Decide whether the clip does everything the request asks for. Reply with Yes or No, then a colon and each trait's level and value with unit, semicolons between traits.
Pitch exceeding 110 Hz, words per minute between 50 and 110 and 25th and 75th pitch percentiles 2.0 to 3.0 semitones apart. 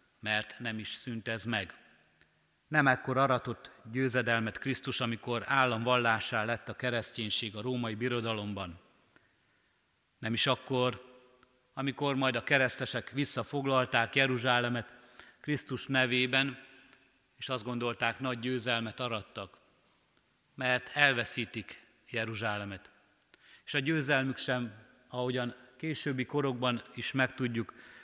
Yes: low, 125 Hz; slow, 105 wpm; narrow, 2.4 semitones